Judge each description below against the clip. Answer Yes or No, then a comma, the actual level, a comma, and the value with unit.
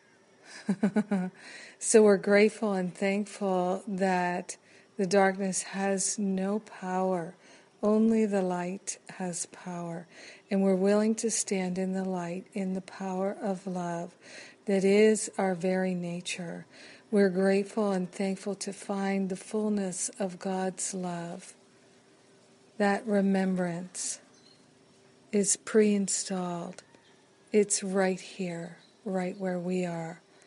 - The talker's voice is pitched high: Yes, high, 195 Hz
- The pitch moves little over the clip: Yes, narrow, 1.7 semitones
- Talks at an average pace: No, slow, 110 wpm